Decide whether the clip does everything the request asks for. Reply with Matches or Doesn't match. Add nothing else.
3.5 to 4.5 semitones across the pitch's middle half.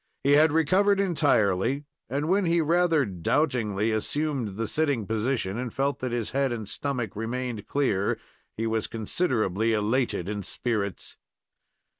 Doesn't match